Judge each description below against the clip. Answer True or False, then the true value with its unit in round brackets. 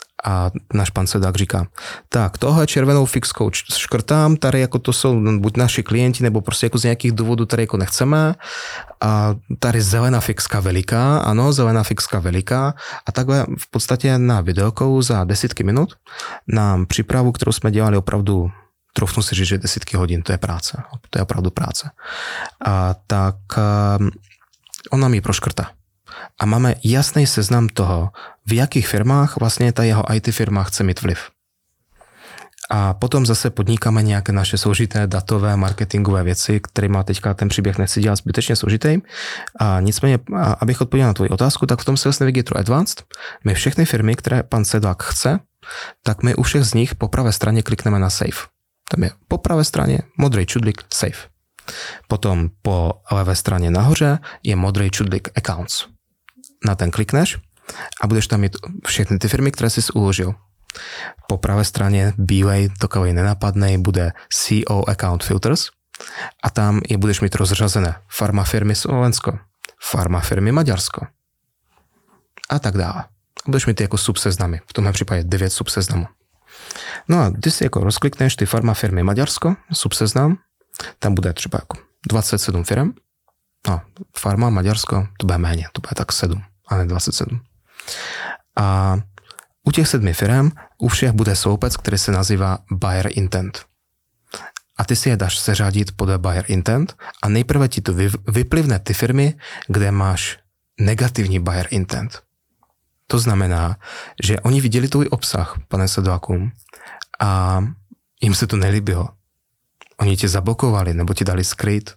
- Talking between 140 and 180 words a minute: True (155 wpm)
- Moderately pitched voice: False (105 Hz)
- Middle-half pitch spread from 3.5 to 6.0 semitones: True (3.9 semitones)